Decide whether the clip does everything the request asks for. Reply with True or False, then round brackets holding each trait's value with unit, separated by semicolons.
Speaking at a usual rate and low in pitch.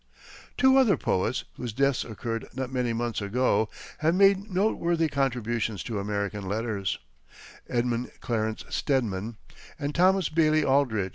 False (130 wpm; 125 Hz)